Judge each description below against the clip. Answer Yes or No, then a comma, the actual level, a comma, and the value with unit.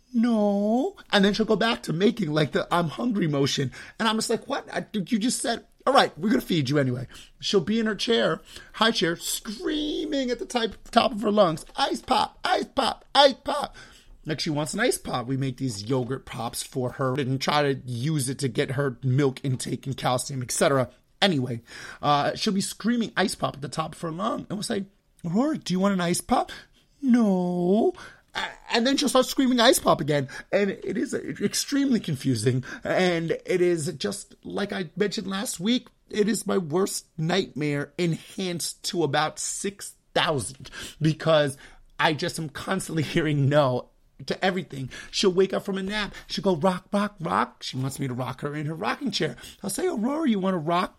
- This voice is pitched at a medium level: Yes, medium, 180 Hz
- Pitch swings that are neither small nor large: No, wide, 7.0 semitones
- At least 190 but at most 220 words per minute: Yes, average, 200 wpm